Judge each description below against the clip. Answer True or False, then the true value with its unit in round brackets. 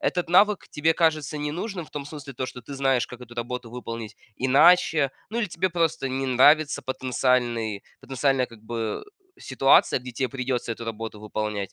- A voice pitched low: True (130 Hz)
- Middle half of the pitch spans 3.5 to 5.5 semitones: True (4.2 semitones)